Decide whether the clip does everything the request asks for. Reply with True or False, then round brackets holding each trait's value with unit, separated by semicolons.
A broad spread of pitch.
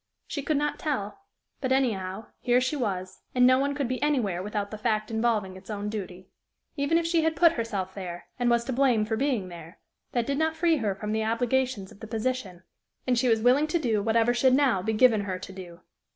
False (4.6 semitones)